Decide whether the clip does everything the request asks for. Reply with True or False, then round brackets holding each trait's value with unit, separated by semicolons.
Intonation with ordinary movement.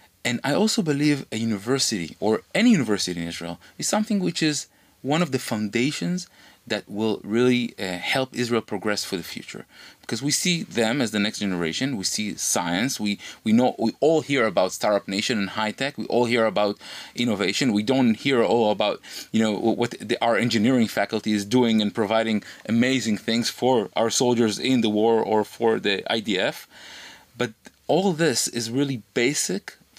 True (4.2 semitones)